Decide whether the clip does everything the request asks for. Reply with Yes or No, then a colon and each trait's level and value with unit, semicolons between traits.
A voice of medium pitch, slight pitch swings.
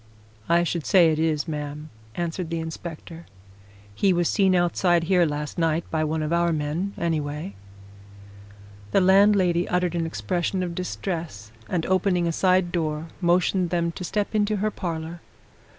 Yes: medium, 170 Hz; narrow, 2.2 semitones